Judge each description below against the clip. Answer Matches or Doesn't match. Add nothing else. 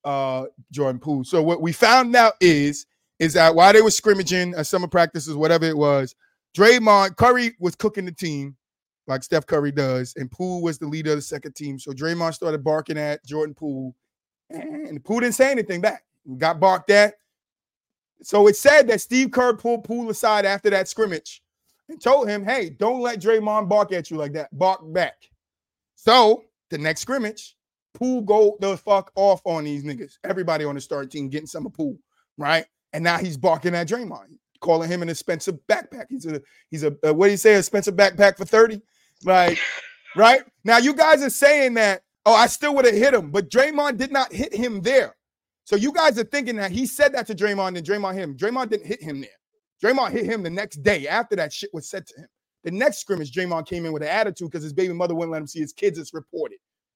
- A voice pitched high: Matches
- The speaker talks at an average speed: Doesn't match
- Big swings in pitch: Matches